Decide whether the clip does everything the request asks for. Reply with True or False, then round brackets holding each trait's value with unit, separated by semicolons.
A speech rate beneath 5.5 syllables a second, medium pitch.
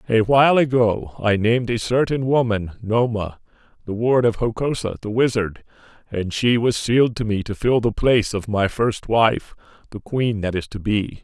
False (4.9 syllables/s; 110 Hz)